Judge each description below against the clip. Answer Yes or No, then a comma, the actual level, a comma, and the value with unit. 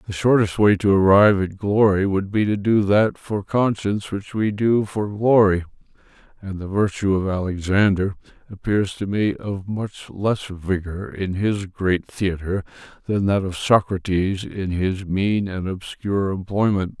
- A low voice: Yes, low, 100 Hz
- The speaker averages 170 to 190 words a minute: No, average, 160 wpm